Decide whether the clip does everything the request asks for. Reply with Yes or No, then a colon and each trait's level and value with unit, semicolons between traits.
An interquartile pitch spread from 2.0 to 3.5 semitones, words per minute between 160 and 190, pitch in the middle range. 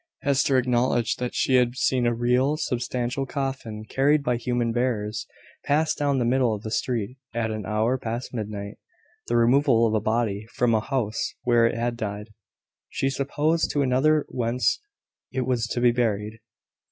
No: average, 2.8 semitones; average, 170 wpm; low, 120 Hz